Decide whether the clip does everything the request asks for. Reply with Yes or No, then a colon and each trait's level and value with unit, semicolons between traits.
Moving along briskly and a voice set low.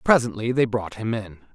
No: average, 195 wpm; low, 110 Hz